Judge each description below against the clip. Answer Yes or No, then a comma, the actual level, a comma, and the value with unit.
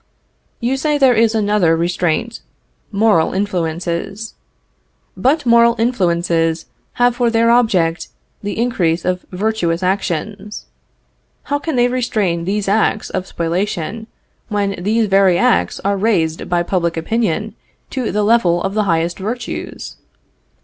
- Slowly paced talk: Yes, slow, 130 wpm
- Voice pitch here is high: Yes, high, 200 Hz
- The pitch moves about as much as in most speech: Yes, average, 4.9 semitones